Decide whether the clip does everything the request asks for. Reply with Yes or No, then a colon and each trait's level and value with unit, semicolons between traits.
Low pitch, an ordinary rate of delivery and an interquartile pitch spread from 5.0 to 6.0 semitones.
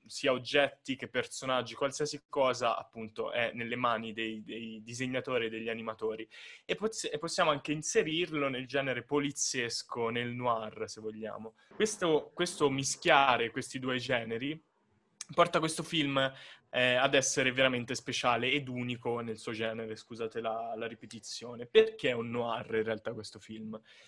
No: low, 125 Hz; average, 145 wpm; average, 3.8 semitones